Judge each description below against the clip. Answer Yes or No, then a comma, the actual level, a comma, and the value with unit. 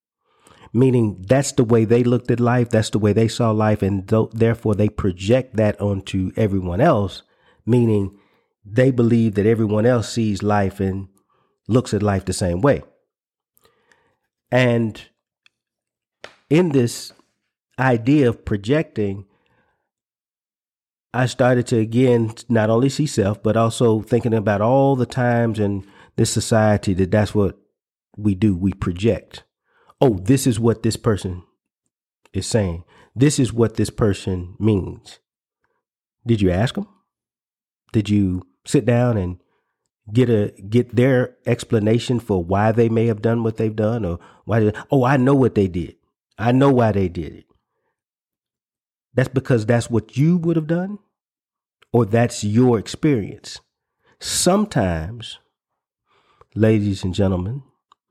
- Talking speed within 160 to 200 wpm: No, average, 140 wpm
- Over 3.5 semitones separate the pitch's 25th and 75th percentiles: No, average, 3.2 semitones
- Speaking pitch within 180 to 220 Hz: No, low, 115 Hz